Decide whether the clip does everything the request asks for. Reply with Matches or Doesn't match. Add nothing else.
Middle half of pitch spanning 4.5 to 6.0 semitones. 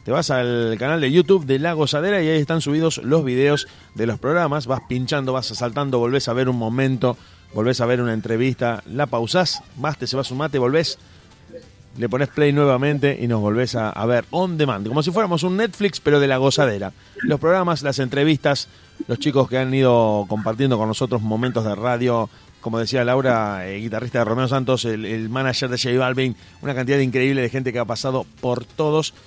Doesn't match